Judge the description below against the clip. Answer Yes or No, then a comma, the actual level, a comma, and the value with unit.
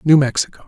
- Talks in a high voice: No, medium, 145 Hz